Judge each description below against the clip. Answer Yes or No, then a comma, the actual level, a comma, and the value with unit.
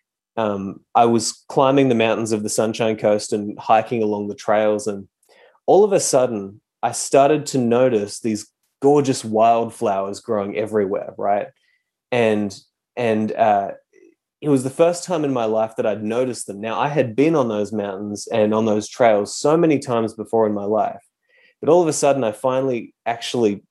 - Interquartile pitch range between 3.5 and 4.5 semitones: Yes, average, 4.0 semitones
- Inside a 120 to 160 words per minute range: No, average, 180 wpm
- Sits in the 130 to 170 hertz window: No, low, 110 Hz